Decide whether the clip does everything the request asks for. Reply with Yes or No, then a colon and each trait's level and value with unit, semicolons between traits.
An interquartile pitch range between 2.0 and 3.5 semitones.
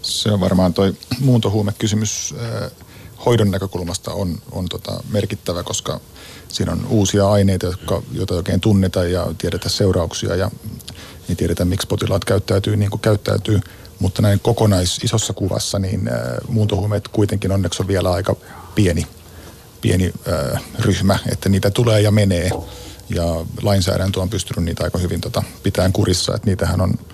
Yes: average, 2.8 semitones